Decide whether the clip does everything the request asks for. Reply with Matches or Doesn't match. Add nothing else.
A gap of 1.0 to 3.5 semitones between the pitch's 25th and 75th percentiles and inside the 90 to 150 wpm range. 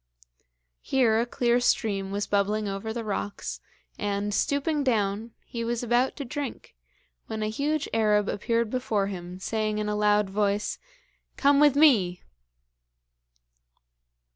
Matches